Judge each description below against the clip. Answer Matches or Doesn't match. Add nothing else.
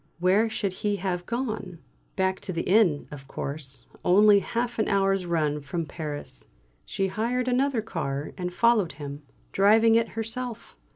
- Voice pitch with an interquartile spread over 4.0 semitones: Matches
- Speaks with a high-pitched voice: Matches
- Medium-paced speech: Matches